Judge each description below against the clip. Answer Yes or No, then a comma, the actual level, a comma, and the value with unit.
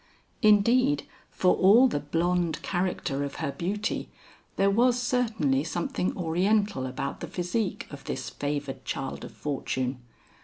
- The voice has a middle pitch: Yes, medium, 180 Hz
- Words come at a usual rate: No, slow, 130 wpm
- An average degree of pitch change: No, wide, 6.8 semitones